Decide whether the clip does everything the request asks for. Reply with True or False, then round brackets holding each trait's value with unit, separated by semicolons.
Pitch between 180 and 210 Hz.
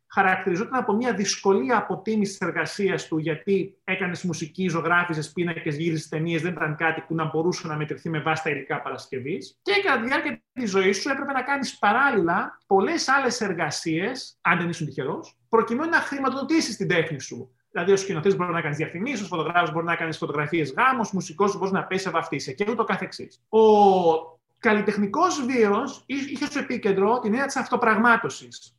True (190 Hz)